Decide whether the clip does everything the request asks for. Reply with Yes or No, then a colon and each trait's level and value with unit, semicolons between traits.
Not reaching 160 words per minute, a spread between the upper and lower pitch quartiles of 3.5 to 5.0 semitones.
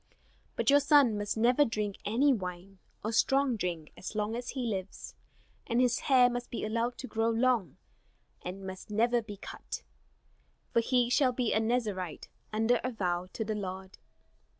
No: average, 175 wpm; average, 3.8 semitones